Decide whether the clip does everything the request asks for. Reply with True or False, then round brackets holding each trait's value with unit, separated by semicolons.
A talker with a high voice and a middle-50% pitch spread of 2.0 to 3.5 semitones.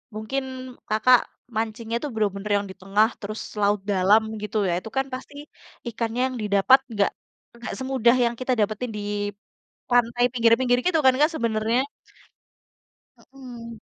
True (230 Hz; 3.0 semitones)